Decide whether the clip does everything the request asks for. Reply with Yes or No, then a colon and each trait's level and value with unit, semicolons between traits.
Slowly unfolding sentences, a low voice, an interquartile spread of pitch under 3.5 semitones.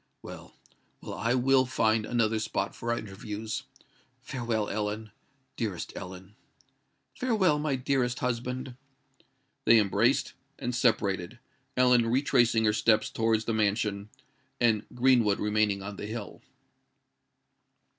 Yes: slow, 105 wpm; low, 115 Hz; average, 2.9 semitones